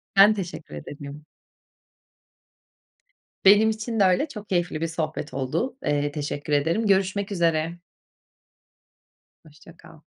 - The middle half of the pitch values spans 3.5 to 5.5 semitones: Yes, average, 5.2 semitones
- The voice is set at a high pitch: No, medium, 170 Hz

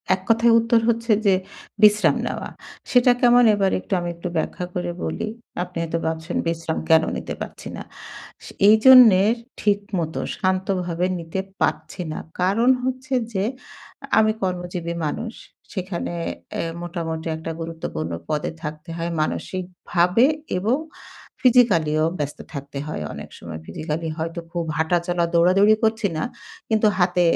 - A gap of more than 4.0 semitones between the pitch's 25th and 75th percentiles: Yes, average, 4.6 semitones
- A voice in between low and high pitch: Yes, medium, 180 Hz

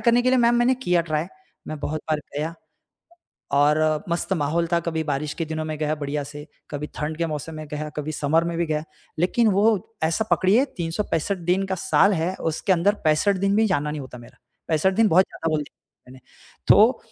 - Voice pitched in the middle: Yes, medium, 160 Hz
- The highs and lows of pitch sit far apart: No, average, 3.9 semitones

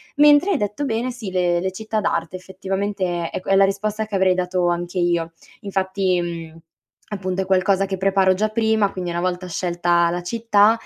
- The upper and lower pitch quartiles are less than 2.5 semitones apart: No, average, 2.8 semitones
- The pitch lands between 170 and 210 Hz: Yes, high, 190 Hz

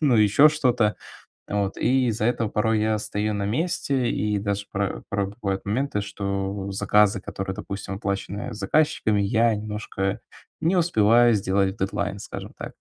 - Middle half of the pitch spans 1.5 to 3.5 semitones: Yes, average, 2.9 semitones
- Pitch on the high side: No, low, 105 Hz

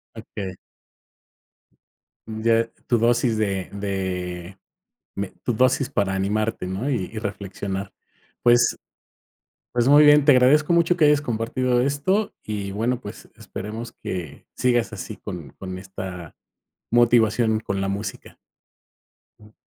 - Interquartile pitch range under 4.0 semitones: No, average, 4.3 semitones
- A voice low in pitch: Yes, low, 110 Hz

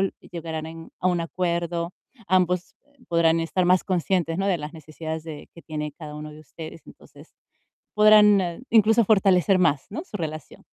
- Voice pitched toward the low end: No, medium, 170 Hz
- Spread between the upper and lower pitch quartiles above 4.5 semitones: No, average, 2.9 semitones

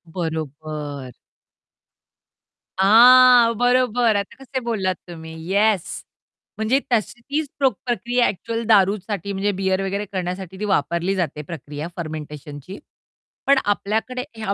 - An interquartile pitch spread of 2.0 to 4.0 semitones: No, wide, 5.6 semitones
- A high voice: Yes, high, 195 Hz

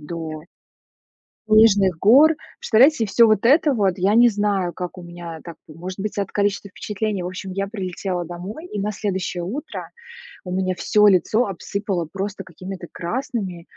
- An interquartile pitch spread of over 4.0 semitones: No, average, 3.1 semitones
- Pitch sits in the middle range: No, high, 195 Hz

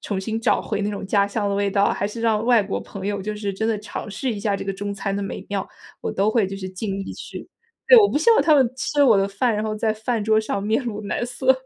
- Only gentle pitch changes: Yes, narrow, 2.3 semitones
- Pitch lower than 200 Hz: No, high, 210 Hz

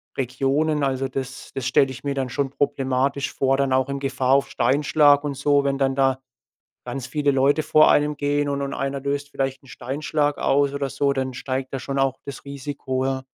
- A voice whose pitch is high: No, low, 135 Hz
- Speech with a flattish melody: Yes, narrow, 1.2 semitones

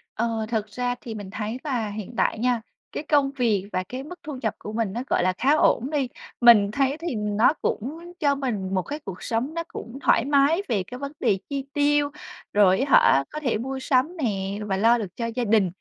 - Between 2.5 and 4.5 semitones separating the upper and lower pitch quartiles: No, average, 5.0 semitones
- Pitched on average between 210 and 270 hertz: Yes, high, 240 Hz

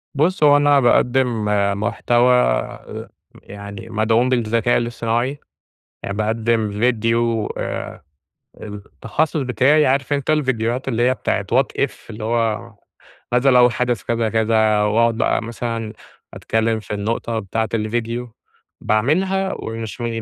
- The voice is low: Yes, low, 115 Hz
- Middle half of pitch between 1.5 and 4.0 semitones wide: Yes, narrow, 2.4 semitones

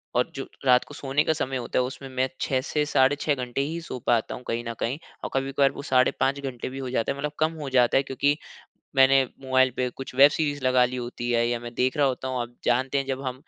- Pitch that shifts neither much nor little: No, narrow, 1.7 semitones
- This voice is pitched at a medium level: No, low, 130 Hz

